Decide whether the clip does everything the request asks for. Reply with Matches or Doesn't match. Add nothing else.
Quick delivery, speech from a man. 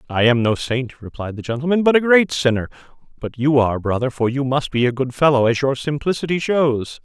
Matches